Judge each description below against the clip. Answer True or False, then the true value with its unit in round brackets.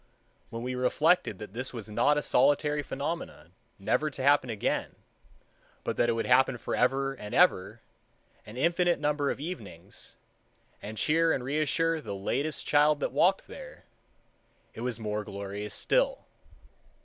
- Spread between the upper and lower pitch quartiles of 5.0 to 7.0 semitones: True (5.3 semitones)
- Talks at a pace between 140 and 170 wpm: True (150 wpm)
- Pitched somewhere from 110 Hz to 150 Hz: True (135 Hz)